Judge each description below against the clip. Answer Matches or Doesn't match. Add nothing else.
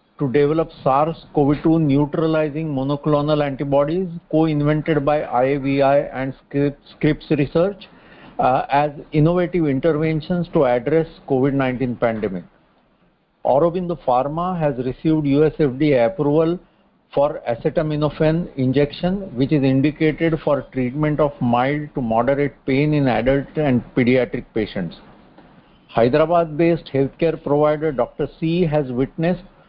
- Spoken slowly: Matches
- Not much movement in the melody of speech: Doesn't match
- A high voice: Doesn't match